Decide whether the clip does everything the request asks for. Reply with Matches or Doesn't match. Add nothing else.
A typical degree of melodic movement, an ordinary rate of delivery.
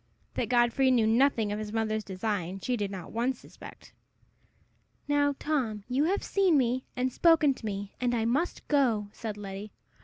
Matches